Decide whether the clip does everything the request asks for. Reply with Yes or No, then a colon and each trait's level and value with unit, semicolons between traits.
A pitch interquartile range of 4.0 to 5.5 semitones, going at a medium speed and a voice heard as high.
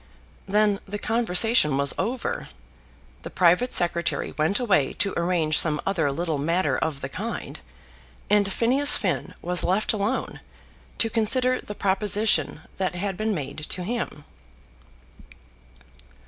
No: average, 4.5 semitones; slow, 130 wpm; high, 195 Hz